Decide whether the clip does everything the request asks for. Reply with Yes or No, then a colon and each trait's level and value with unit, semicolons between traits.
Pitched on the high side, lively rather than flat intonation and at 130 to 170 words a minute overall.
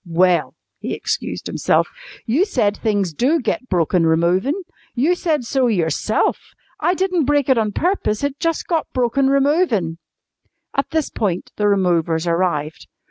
Yes: high, 230 Hz; wide, 8.4 semitones; average, 145 wpm